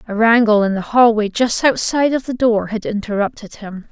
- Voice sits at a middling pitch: No, high, 220 Hz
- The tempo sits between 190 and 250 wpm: Yes, average, 200 wpm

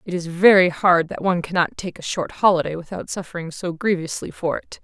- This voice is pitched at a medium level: Yes, medium, 175 Hz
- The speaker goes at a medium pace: No, fast, 210 wpm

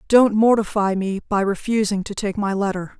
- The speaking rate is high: No, average, 180 wpm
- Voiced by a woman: Yes, female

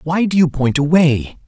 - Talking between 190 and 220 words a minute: Yes, fast, 205 wpm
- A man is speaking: Yes, male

